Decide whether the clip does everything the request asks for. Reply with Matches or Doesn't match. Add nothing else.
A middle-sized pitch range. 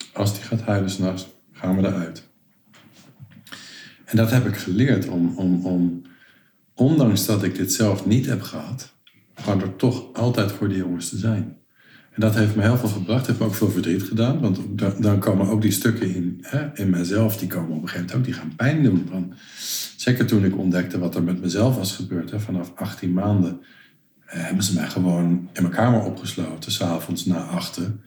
Matches